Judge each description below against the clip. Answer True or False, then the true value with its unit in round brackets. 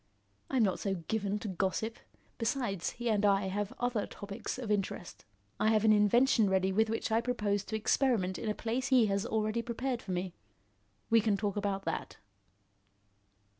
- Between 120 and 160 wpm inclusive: False (175 wpm)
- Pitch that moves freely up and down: False (2.7 semitones)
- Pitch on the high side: True (210 Hz)